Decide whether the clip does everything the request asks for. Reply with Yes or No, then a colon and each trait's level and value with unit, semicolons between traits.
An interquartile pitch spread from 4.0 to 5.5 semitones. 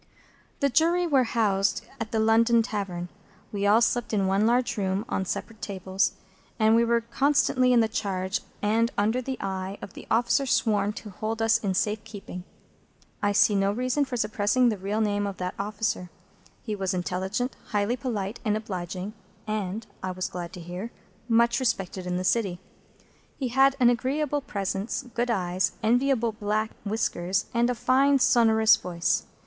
No: average, 3.4 semitones